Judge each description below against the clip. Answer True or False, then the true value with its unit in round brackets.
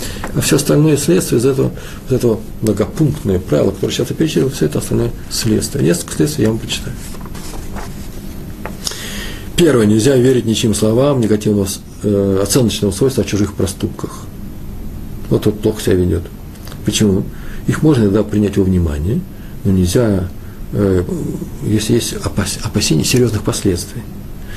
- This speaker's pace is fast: False (135 wpm)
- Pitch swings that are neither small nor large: True (3.0 semitones)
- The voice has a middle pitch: False (105 Hz)